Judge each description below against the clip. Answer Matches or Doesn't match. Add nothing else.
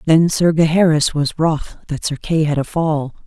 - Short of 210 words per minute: Matches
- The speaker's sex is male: Doesn't match